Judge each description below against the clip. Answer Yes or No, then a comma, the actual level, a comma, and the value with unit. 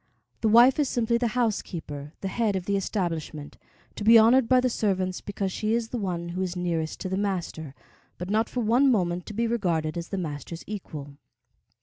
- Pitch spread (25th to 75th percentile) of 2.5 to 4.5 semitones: No, average, 4.9 semitones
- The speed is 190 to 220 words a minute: Yes, fast, 205 wpm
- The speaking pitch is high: Yes, high, 195 Hz